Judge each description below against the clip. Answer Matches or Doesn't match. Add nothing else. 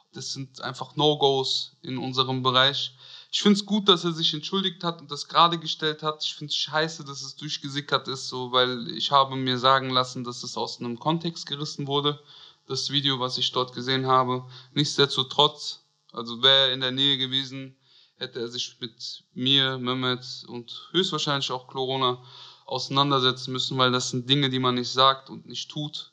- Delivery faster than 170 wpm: Matches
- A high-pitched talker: Doesn't match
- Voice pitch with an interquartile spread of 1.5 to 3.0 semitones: Matches